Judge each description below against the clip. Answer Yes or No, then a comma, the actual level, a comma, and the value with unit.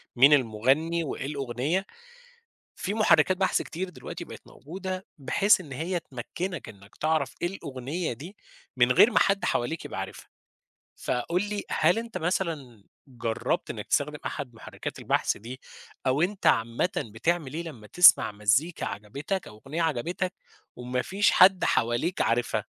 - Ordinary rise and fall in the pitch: No, wide, 6.7 semitones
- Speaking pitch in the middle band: Yes, medium, 155 Hz